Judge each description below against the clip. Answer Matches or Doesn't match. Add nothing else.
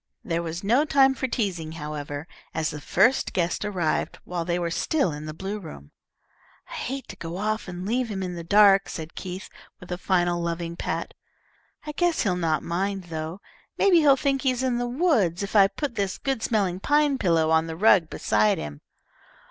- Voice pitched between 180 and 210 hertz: Matches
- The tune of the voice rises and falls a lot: Matches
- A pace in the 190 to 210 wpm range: Matches